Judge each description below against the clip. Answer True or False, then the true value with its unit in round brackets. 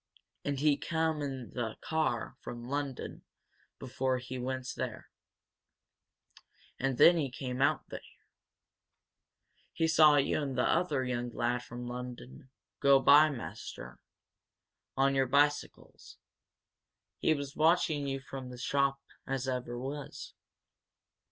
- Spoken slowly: True (120 wpm)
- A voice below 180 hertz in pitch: True (135 Hz)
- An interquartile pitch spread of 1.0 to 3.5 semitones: True (2.5 semitones)